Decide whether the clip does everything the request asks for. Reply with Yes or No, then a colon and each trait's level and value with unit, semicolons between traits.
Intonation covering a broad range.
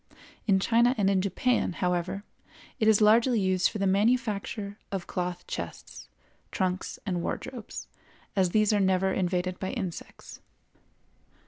No: average, 2.7 semitones